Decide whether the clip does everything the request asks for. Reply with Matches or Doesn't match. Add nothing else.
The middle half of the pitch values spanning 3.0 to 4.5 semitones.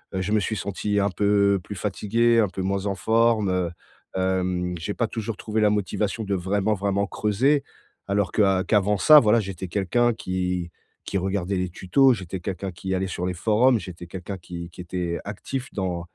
Doesn't match